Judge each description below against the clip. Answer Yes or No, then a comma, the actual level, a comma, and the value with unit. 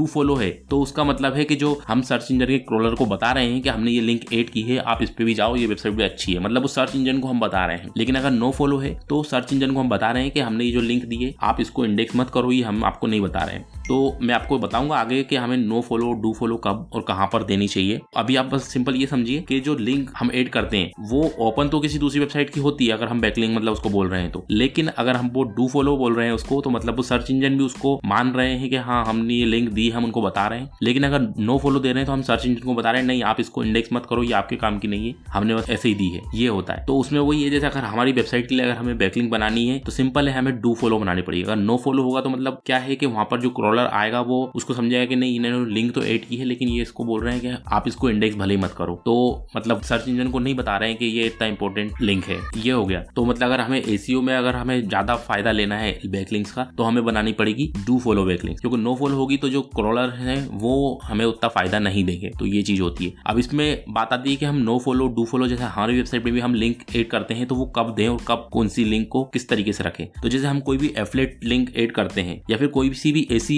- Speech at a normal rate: No, fast, 240 wpm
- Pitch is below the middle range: Yes, low, 120 Hz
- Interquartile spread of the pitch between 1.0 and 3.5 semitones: Yes, average, 2.9 semitones